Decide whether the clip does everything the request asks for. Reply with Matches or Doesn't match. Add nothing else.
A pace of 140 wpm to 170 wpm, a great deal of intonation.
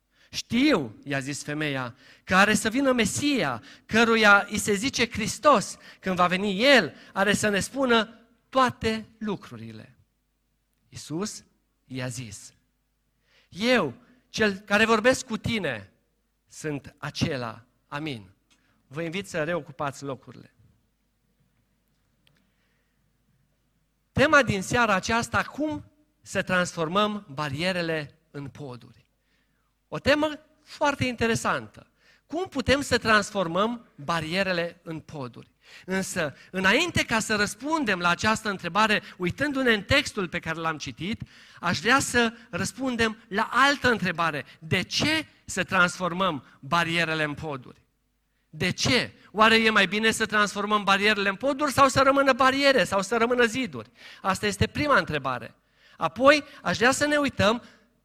Doesn't match